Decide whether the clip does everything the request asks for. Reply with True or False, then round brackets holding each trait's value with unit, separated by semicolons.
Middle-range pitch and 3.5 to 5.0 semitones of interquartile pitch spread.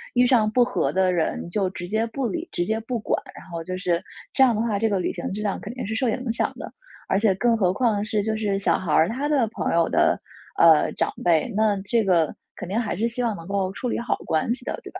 False (210 Hz; 4.0 semitones)